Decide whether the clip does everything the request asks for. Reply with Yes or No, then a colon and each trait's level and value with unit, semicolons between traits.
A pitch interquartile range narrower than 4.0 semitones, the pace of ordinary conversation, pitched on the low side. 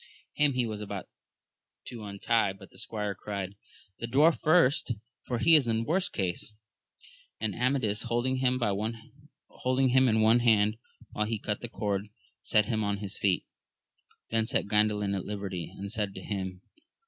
Yes: average, 3.4 semitones; average, 160 wpm; low, 110 Hz